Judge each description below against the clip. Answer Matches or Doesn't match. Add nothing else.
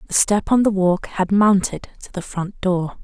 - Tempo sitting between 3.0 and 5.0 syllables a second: Matches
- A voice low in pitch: Doesn't match